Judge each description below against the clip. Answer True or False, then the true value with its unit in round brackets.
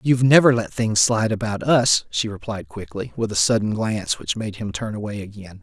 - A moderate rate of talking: False (215 wpm)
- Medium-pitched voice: False (110 Hz)